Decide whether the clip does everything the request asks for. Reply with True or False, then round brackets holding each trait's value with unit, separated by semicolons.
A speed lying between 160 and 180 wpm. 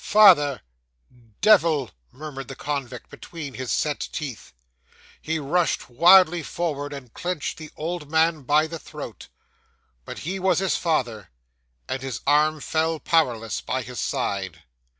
False (135 wpm)